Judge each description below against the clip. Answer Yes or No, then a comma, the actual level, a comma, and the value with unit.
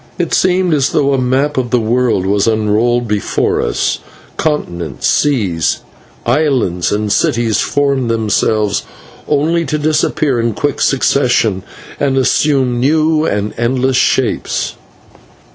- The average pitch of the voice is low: Yes, low, 125 Hz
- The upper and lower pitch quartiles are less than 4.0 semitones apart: No, average, 5.2 semitones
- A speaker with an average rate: No, slow, 125 wpm